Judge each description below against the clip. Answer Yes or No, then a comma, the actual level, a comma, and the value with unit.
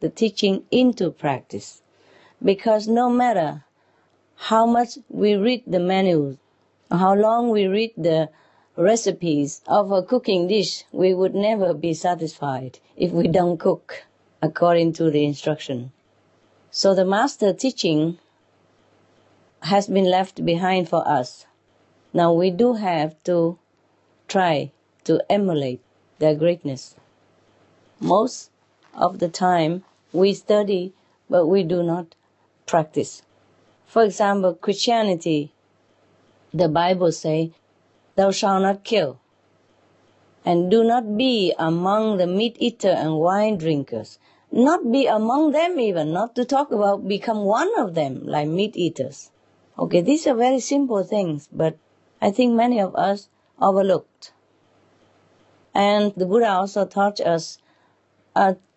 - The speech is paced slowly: Yes, slow, 125 wpm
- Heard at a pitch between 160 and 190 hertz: Yes, medium, 185 Hz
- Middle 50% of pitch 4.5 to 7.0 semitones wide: Yes, average, 5.1 semitones